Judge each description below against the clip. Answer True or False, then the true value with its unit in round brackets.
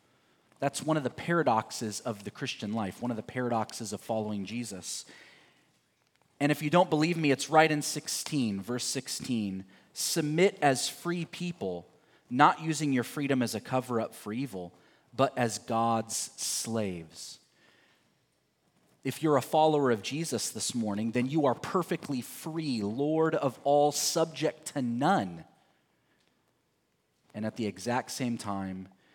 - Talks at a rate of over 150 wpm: False (145 wpm)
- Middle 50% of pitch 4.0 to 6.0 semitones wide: True (5.5 semitones)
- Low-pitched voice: True (125 Hz)